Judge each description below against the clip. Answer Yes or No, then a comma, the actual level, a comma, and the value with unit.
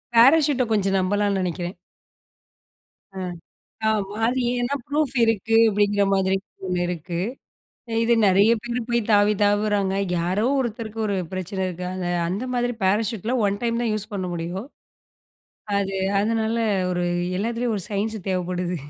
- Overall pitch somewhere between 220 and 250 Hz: No, high, 205 Hz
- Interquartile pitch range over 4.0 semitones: No, average, 3.3 semitones